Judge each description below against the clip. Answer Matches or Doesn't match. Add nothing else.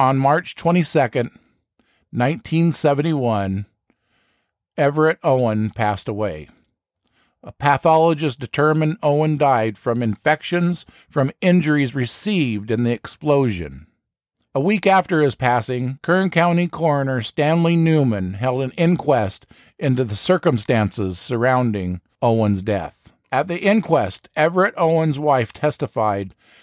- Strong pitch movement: Matches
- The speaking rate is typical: Doesn't match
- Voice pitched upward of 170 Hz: Doesn't match